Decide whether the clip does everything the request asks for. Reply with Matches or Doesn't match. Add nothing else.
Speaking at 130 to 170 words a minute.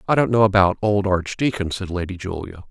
Doesn't match